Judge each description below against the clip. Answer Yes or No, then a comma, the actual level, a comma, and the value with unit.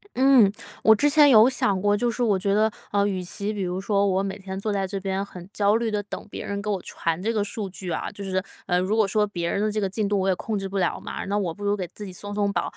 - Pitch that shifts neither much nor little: No, narrow, 1.8 semitones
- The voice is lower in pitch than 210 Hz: Yes, high, 200 Hz